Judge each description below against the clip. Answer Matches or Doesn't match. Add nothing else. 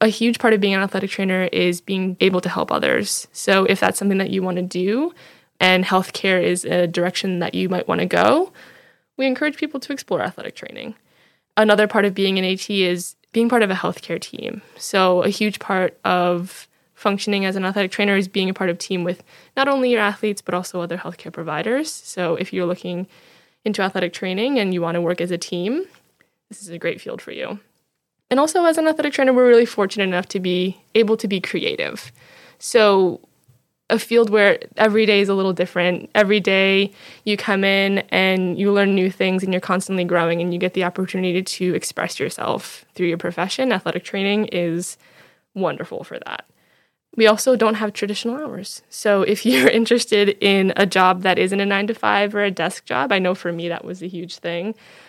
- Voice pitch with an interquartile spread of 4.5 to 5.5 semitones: Doesn't match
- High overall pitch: Matches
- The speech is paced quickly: Matches